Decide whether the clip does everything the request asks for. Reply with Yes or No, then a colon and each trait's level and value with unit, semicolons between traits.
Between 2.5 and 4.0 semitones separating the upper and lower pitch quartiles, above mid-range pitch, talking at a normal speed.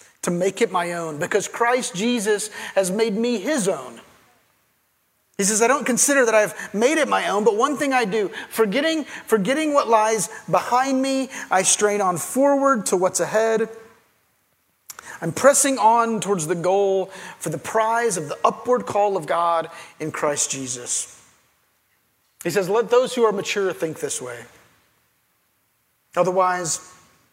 No: average, 4.8 semitones; high, 215 Hz; average, 155 wpm